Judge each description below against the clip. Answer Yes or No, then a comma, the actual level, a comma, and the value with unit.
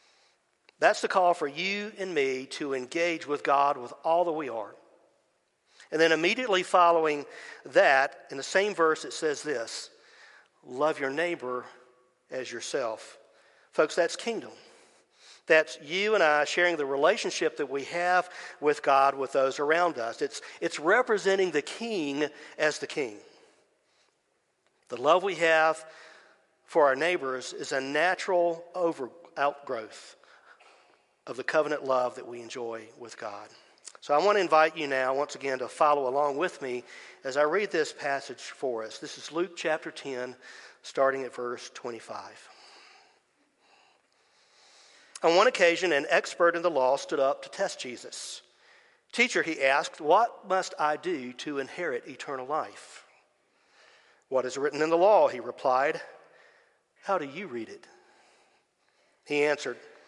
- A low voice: No, medium, 160 Hz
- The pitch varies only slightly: No, wide, 5.4 semitones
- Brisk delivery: No, average, 150 wpm